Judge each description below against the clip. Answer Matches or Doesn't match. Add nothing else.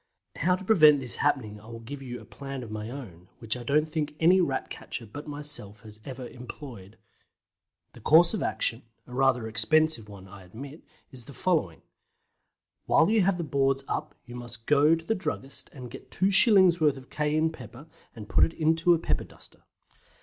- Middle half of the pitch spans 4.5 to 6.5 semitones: Matches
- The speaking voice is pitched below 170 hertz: Matches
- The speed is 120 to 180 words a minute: Doesn't match